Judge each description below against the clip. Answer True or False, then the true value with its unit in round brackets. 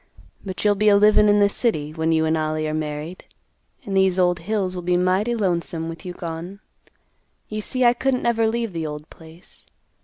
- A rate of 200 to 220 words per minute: True (205 wpm)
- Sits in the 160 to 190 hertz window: True (185 Hz)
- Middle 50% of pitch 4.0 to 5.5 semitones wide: True (4.5 semitones)